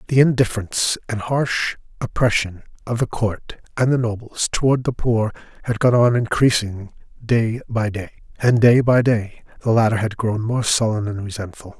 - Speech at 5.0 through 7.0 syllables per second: No, 4.8 syllables/s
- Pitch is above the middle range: No, low, 115 Hz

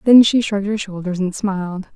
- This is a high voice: Yes, high, 200 Hz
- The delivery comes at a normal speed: No, fast, 215 wpm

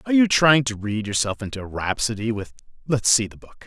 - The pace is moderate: No, fast, 215 wpm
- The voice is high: No, low, 115 Hz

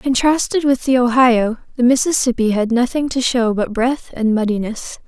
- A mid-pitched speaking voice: No, high, 245 Hz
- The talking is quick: No, average, 165 wpm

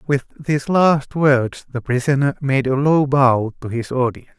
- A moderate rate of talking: Yes, average, 180 wpm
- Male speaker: Yes, male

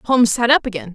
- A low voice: No, high, 230 Hz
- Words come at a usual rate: No, fast, 255 wpm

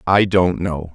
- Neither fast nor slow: Yes, average, 190 wpm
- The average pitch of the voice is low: Yes, very low, 90 Hz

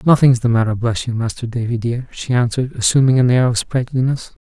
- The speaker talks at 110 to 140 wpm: No, fast, 205 wpm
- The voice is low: Yes, low, 120 Hz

